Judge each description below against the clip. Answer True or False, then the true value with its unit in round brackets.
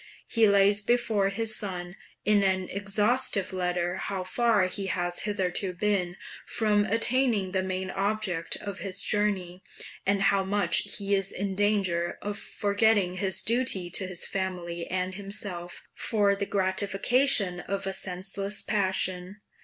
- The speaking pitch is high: True (195 Hz)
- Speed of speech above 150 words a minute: False (140 wpm)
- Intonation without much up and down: True (2.0 semitones)